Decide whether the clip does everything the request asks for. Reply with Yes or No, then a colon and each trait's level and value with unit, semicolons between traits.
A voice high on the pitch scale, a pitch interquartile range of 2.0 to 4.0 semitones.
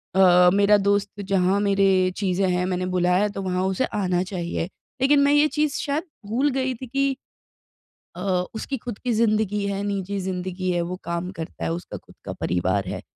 Yes: high, 195 Hz; average, 3.3 semitones